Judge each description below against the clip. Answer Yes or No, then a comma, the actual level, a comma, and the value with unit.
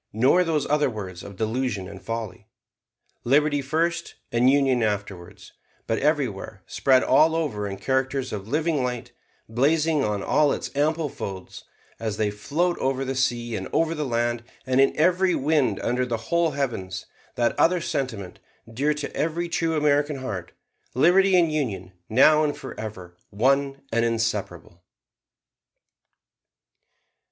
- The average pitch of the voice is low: Yes, low, 130 Hz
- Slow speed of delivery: No, average, 145 wpm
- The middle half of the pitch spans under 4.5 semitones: No, wide, 5.6 semitones